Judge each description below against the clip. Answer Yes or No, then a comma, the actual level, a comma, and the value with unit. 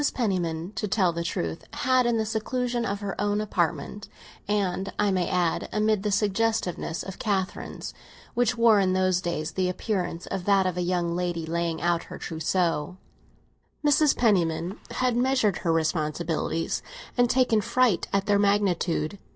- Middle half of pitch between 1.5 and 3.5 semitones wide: No, average, 3.9 semitones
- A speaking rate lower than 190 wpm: Yes, average, 150 wpm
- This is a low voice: No, high, 190 Hz